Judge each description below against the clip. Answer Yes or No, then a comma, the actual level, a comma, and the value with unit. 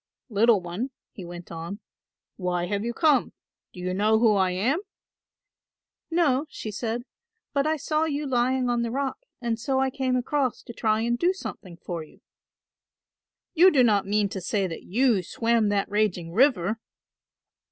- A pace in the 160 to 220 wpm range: Yes, average, 170 wpm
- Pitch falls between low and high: No, high, 225 Hz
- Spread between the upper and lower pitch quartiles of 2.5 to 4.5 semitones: No, average, 5.2 semitones